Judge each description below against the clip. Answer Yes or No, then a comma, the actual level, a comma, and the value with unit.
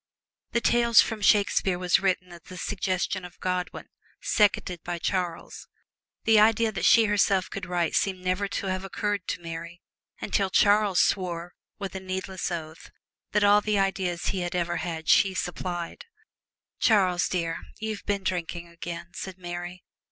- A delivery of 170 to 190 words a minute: No, average, 155 wpm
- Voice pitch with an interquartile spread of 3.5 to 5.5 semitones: No, narrow, 2.5 semitones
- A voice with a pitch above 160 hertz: Yes, medium, 185 Hz